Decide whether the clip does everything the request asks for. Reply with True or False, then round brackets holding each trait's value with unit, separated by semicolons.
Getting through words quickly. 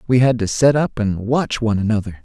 True (240 wpm)